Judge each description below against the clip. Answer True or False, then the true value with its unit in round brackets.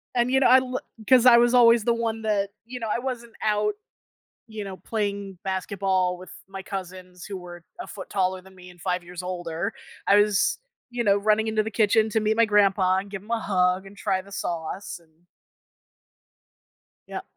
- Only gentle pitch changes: False (3.2 semitones)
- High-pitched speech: True (200 Hz)